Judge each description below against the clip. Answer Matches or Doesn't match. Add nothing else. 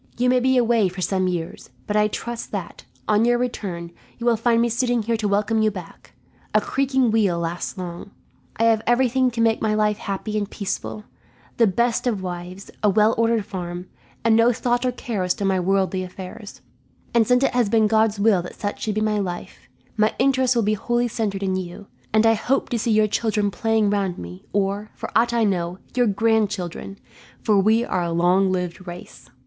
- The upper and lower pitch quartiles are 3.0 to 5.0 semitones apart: Matches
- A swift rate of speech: Matches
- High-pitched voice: Matches